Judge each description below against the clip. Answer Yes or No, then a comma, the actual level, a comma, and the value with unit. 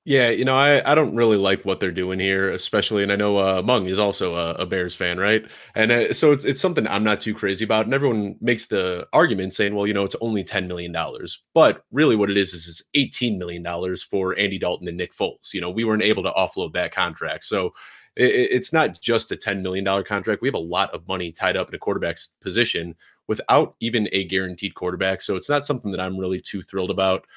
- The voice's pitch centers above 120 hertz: No, low, 100 Hz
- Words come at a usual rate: No, fast, 240 wpm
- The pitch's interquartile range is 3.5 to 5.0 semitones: Yes, average, 4.0 semitones